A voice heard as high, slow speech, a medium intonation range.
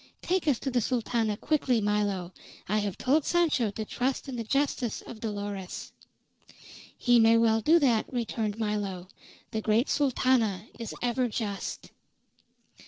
No: high, 230 Hz; average, 145 wpm; average, 3.5 semitones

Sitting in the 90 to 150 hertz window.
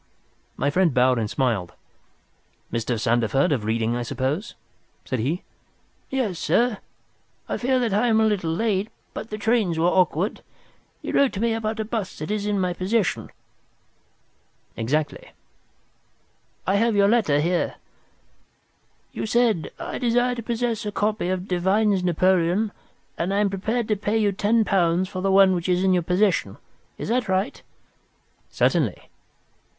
No: high, 190 Hz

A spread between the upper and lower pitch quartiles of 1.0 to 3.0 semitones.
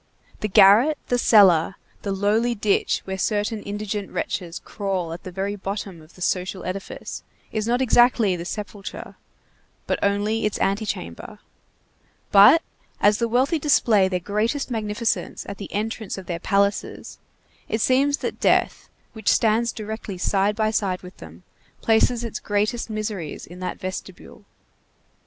Yes: average, 2.7 semitones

